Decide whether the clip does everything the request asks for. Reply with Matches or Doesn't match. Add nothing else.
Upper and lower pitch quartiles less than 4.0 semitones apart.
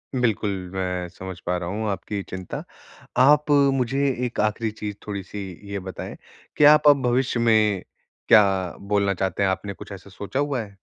Doesn't match